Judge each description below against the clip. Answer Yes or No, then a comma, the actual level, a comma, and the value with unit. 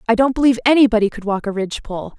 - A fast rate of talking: Yes, fast, 220 wpm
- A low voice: No, high, 230 Hz